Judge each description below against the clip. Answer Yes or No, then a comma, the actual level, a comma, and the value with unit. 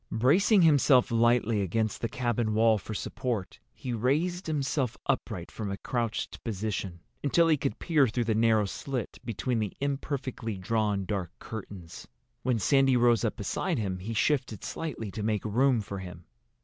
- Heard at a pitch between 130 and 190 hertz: No, low, 115 Hz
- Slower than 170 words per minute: Yes, average, 160 wpm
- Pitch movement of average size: Yes, average, 4.2 semitones